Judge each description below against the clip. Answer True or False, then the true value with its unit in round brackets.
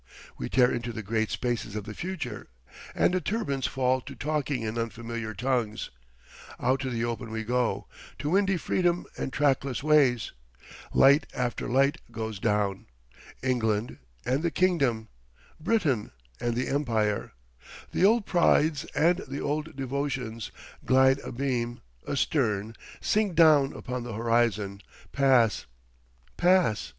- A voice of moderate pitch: False (125 Hz)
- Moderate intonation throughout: True (4.5 semitones)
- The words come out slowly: True (130 wpm)